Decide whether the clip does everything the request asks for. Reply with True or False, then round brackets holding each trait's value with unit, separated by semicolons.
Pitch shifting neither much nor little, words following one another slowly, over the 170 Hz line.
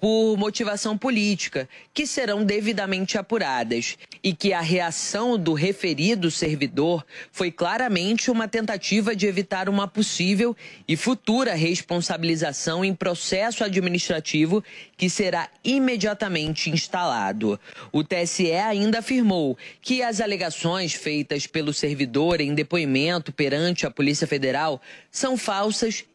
True (4.9 semitones; 115 wpm; 185 Hz)